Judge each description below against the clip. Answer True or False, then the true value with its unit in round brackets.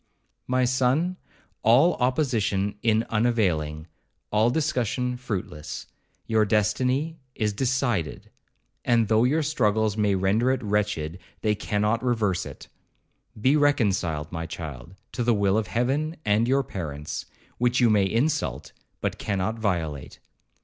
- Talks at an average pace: False (130 wpm)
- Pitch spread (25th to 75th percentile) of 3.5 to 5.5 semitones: True (4.2 semitones)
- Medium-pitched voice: False (110 Hz)